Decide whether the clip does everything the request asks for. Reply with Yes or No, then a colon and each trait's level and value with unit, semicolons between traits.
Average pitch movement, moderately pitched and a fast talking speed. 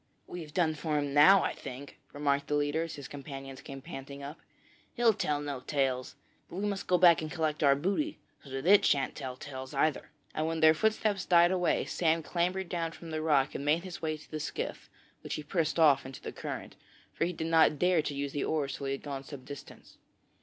Yes: average, 3.4 semitones; medium, 155 Hz; fast, 225 wpm